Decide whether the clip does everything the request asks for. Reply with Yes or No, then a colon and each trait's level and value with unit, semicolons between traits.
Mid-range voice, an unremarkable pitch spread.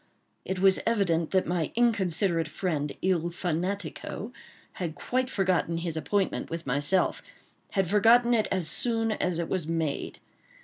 Yes: medium, 180 Hz; average, 3.5 semitones